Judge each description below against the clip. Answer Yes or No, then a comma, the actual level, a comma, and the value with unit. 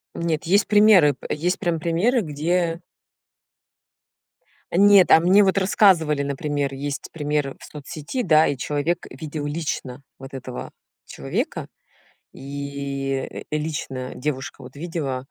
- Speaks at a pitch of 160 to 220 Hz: No, medium, 150 Hz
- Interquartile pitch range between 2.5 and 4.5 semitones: Yes, average, 3.6 semitones